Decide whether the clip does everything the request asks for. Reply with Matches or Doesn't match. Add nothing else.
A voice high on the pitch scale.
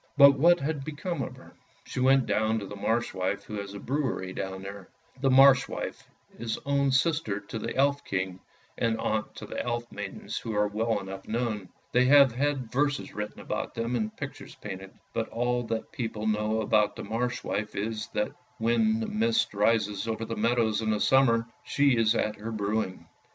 Doesn't match